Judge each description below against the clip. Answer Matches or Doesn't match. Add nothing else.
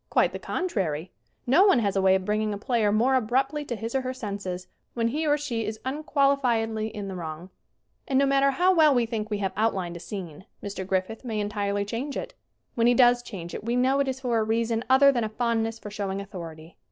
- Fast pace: Matches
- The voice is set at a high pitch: Matches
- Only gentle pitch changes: Doesn't match